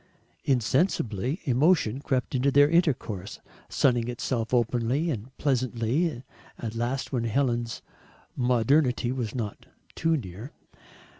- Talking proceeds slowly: Yes, slow, 105 wpm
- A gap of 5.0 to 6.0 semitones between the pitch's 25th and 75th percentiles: No, average, 3.3 semitones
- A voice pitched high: No, low, 125 Hz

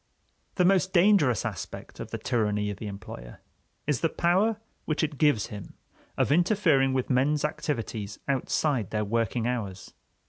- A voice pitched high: No, low, 130 Hz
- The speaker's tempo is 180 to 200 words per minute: No, average, 150 wpm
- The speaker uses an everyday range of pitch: No, wide, 6.9 semitones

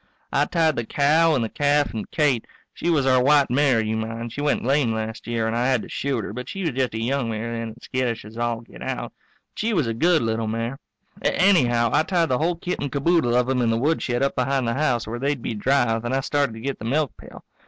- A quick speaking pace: Yes, fast, 260 wpm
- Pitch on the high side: No, low, 125 Hz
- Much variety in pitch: No, average, 3.9 semitones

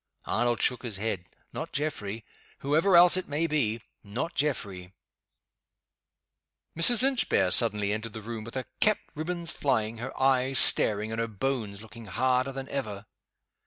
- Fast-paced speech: No, average, 155 wpm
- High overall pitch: No, low, 120 Hz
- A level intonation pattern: No, average, 5.1 semitones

